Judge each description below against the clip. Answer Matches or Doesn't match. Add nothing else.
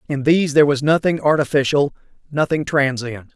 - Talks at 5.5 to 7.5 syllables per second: Matches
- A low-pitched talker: Doesn't match